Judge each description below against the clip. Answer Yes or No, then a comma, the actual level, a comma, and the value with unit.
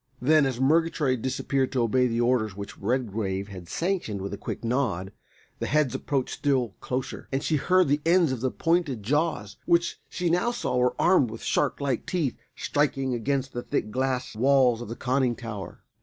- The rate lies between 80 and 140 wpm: No, average, 190 wpm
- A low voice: Yes, low, 130 Hz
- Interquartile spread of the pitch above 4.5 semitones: No, average, 4.2 semitones